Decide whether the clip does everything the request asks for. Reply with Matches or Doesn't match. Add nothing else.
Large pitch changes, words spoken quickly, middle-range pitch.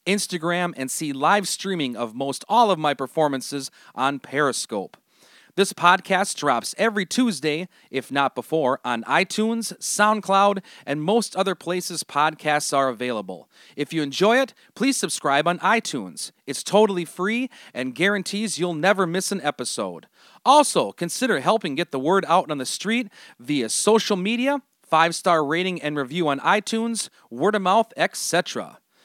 Doesn't match